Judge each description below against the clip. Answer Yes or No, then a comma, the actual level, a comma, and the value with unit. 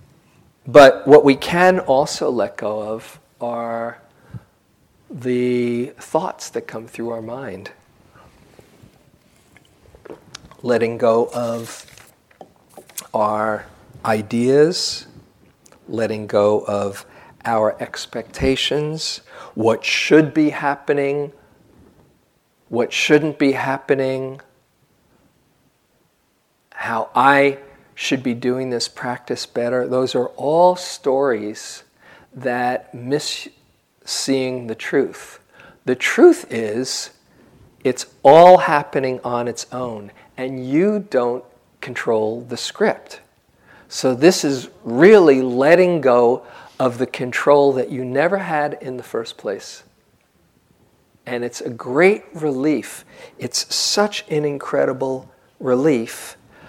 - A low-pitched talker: Yes, low, 130 Hz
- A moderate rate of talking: No, slow, 100 wpm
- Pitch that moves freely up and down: No, average, 3.3 semitones